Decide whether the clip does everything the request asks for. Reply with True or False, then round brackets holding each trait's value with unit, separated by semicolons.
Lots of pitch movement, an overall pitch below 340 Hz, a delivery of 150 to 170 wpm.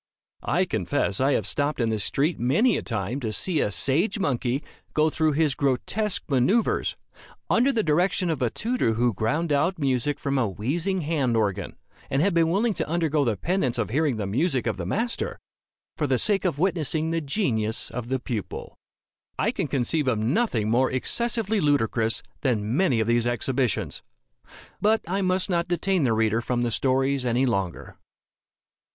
False (6.6 semitones; 140 Hz; 180 wpm)